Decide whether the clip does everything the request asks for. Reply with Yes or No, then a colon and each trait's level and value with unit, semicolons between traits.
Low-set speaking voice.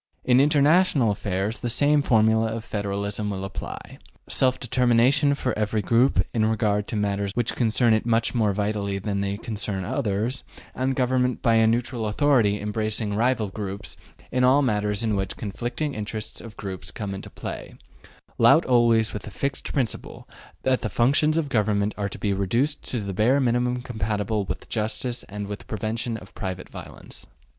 Yes: low, 110 Hz